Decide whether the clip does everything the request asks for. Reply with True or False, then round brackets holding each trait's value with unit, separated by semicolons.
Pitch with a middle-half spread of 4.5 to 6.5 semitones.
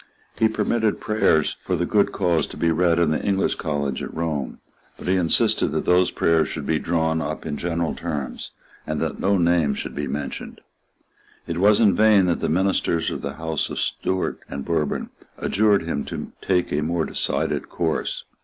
False (3.1 semitones)